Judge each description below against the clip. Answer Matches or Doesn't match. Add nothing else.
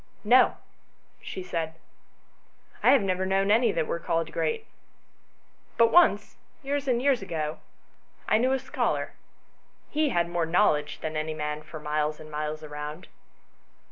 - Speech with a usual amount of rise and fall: Doesn't match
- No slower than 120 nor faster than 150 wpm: Matches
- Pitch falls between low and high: Matches